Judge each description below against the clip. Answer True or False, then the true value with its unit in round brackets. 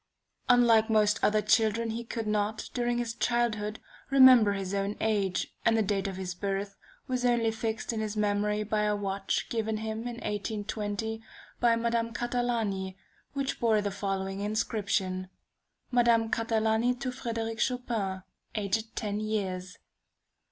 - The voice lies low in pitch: False (220 Hz)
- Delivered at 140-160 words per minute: True (145 wpm)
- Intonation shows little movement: True (2.2 semitones)